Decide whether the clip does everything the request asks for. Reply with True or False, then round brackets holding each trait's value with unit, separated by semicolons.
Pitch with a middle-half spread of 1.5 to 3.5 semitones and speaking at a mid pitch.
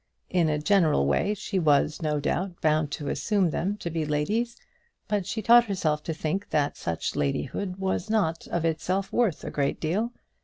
False (4.9 semitones; 170 Hz)